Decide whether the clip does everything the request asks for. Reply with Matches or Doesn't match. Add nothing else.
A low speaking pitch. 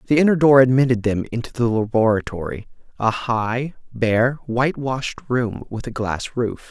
Matches